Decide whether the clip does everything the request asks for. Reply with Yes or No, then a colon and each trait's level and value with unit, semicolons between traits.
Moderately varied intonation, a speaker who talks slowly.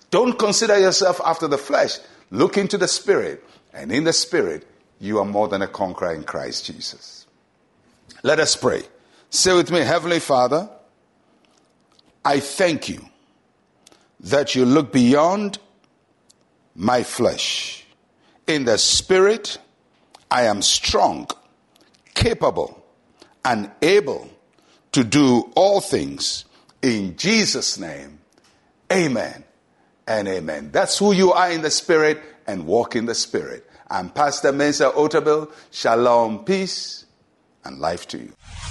No: wide, 7.0 semitones; slow, 125 wpm